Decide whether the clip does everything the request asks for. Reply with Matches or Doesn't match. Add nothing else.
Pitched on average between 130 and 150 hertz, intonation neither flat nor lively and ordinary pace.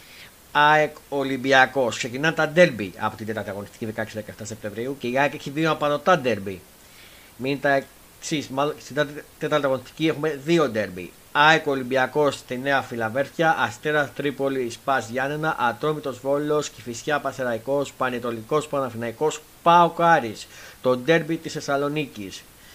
Matches